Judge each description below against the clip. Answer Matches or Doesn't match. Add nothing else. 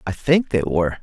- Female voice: Doesn't match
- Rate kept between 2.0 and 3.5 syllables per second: Doesn't match